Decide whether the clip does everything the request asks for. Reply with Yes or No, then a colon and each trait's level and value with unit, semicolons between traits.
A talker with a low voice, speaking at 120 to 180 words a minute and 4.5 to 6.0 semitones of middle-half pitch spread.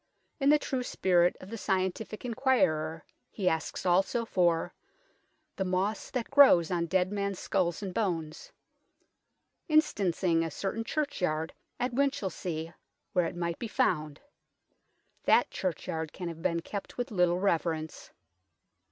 No: medium, 185 Hz; slow, 135 wpm; average, 4.9 semitones